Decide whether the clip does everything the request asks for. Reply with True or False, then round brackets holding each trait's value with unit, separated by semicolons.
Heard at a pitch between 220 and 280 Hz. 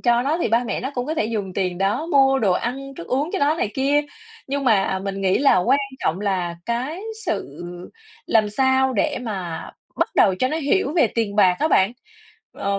True (240 Hz)